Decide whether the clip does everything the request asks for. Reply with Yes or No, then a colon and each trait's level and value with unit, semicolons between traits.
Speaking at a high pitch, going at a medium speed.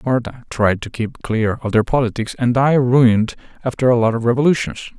No: low, 120 Hz; average, 195 wpm